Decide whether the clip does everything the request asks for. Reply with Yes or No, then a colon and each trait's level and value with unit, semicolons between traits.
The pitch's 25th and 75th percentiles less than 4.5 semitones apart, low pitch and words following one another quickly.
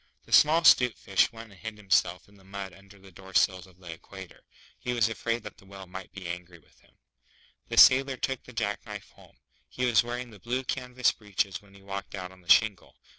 Yes: average, 3.9 semitones; low, 100 Hz; fast, 225 wpm